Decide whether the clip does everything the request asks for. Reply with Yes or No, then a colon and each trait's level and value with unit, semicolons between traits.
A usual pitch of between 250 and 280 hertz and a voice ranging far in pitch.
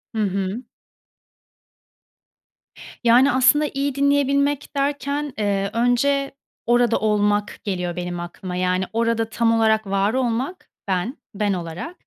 No: high, 230 Hz; wide, 5.8 semitones